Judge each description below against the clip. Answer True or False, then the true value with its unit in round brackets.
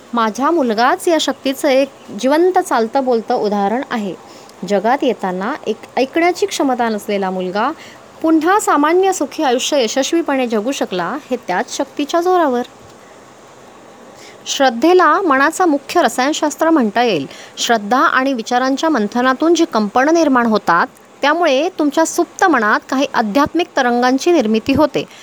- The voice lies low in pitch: False (270 Hz)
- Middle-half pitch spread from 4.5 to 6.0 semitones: True (5.2 semitones)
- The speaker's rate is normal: True (120 wpm)